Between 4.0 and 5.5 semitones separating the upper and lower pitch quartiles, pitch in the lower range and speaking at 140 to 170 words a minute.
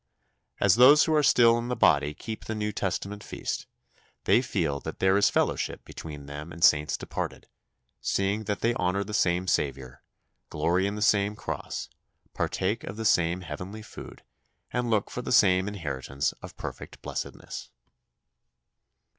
Yes: average, 4.7 semitones; low, 100 Hz; average, 160 wpm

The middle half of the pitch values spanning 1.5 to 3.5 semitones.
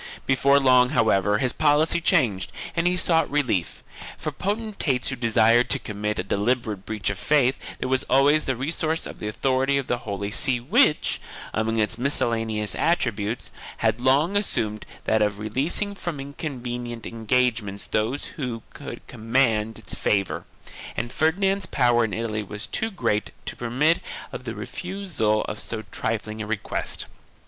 No: average, 5.1 semitones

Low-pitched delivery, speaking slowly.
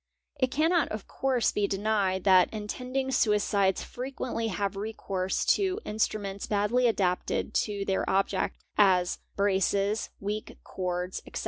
No: high, 205 Hz; slow, 125 wpm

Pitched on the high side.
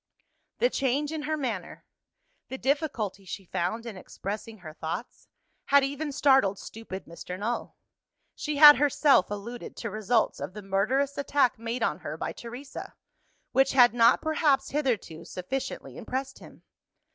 Yes: high, 245 Hz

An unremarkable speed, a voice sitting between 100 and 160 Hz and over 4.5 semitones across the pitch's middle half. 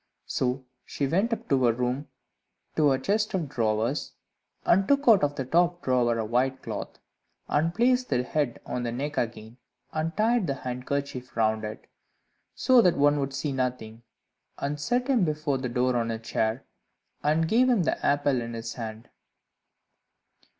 Yes: average, 170 wpm; low, 135 Hz; wide, 5.4 semitones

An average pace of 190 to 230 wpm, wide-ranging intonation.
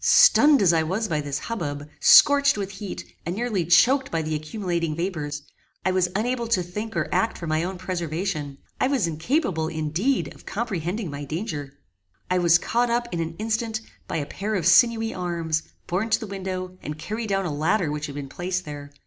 Yes: average, 200 wpm; wide, 5.7 semitones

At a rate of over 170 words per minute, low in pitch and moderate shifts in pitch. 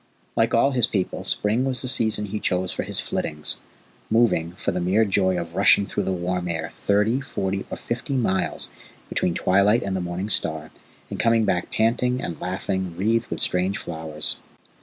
Yes: average, 185 wpm; very low, 95 Hz; average, 4.2 semitones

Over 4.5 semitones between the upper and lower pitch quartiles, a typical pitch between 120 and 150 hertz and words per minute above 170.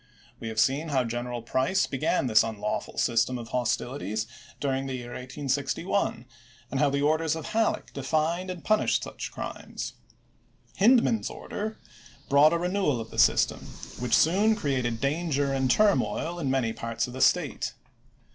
No: average, 5.3 semitones; low, 135 Hz; average, 155 wpm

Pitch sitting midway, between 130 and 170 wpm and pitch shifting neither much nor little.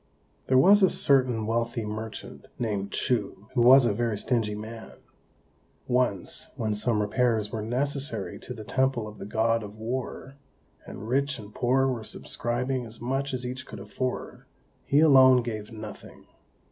No: low, 120 Hz; average, 160 wpm; average, 3.2 semitones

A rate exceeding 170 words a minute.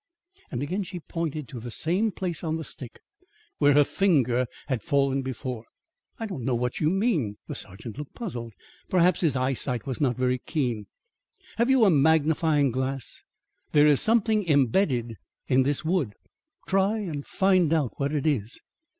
No: average, 165 wpm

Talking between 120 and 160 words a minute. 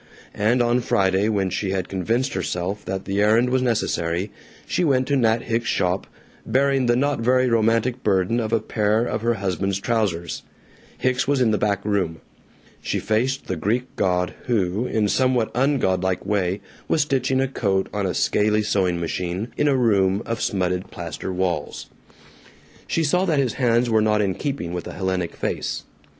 No: average, 180 wpm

